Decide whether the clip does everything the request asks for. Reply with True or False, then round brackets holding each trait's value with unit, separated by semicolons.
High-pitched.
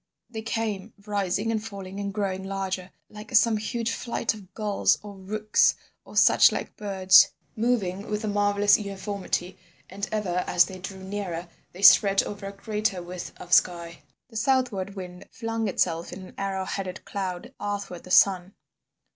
True (200 Hz)